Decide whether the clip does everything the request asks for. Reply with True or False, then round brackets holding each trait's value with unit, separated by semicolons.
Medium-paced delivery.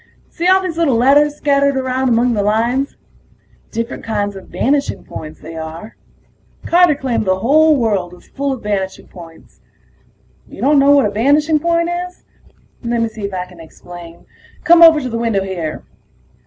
True (170 wpm)